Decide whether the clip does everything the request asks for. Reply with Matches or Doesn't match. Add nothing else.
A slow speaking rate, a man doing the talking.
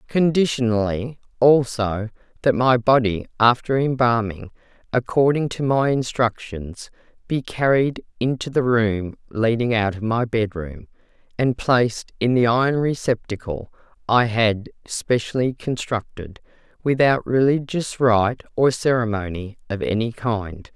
Doesn't match